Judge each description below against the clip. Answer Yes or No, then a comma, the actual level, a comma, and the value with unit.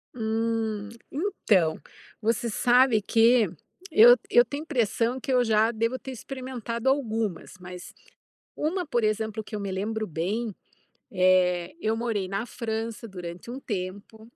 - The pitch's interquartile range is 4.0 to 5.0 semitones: No, average, 3.0 semitones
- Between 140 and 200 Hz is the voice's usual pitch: No, high, 225 Hz